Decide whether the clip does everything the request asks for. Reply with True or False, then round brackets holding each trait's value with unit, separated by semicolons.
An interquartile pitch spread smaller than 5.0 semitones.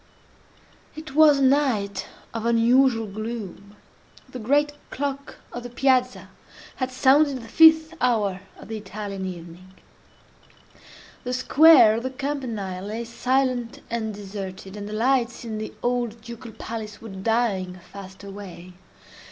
True (4.2 semitones)